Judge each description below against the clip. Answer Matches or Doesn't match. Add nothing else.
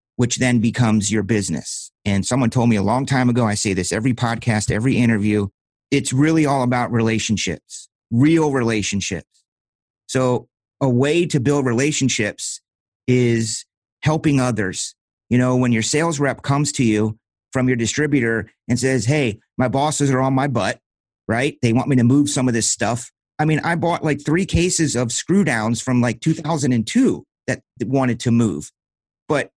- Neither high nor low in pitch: Doesn't match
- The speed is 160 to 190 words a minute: Matches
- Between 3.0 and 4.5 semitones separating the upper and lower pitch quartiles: Matches